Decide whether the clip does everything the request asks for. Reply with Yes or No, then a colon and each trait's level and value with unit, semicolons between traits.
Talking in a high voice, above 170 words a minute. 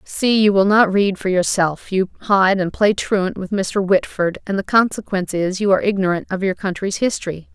Yes: high, 195 Hz; fast, 205 wpm